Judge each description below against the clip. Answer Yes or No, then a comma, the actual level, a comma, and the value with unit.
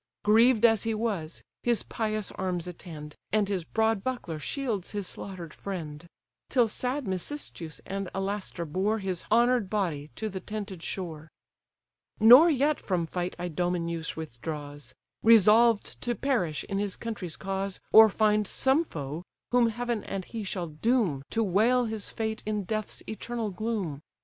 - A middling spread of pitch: Yes, average, 4.3 semitones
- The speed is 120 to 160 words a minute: Yes, average, 150 wpm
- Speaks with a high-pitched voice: Yes, high, 205 Hz